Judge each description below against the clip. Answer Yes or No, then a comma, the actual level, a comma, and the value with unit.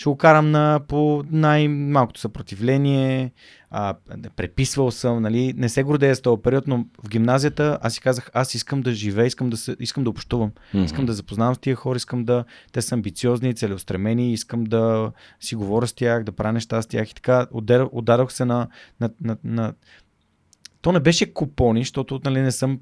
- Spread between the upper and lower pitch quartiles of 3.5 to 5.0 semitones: No, average, 2.8 semitones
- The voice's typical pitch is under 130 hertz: Yes, low, 120 Hz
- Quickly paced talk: Yes, fast, 190 wpm